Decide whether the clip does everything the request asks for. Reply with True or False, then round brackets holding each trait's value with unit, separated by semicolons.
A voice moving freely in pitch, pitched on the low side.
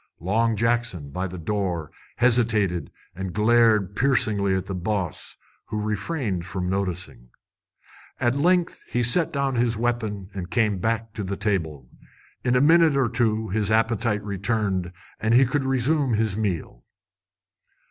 False (4.0 semitones; 110 Hz)